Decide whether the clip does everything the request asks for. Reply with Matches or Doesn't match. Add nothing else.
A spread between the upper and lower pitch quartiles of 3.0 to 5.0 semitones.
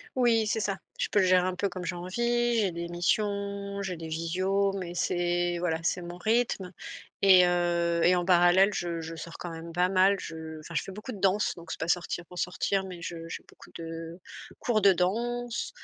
Doesn't match